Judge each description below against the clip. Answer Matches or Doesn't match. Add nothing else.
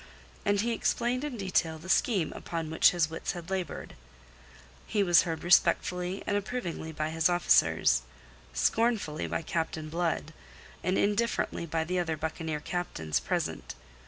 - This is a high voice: Doesn't match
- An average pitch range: Matches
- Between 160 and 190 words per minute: Doesn't match